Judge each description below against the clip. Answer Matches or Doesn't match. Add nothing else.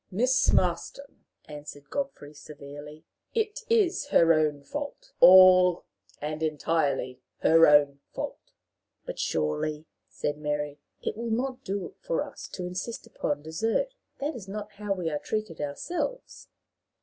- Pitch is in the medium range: Matches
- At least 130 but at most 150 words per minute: Matches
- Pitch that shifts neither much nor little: Doesn't match